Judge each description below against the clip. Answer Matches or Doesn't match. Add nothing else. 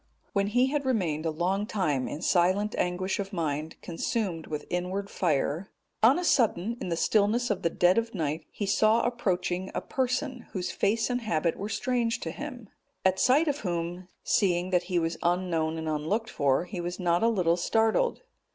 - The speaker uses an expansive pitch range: Doesn't match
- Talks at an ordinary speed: Matches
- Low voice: Doesn't match